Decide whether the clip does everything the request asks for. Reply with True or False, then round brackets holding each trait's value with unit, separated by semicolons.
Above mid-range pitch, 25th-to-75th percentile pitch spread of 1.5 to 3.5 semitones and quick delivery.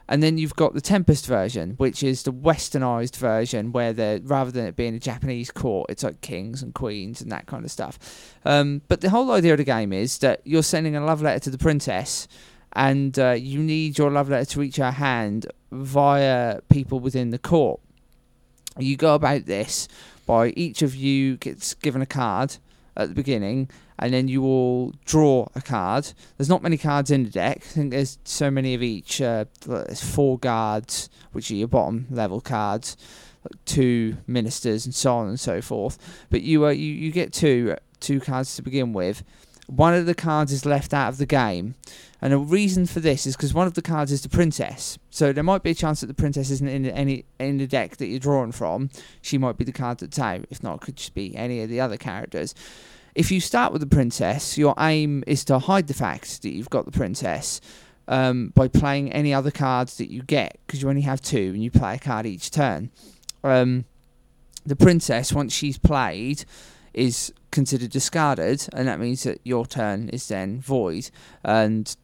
False (135 Hz; 2.9 semitones; 210 wpm)